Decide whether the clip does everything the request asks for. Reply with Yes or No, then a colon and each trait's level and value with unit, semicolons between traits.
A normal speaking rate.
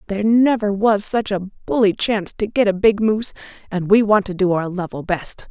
No: fast, 220 wpm